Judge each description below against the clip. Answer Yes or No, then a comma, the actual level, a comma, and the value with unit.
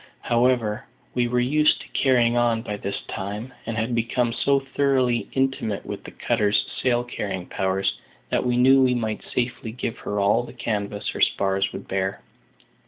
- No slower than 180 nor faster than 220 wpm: No, average, 170 wpm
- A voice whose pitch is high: No, low, 120 Hz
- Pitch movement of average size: Yes, average, 3.2 semitones